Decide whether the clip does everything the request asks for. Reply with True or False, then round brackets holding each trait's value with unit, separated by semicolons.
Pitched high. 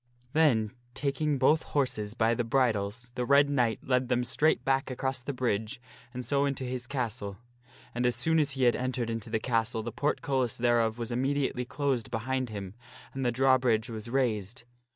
False (125 Hz)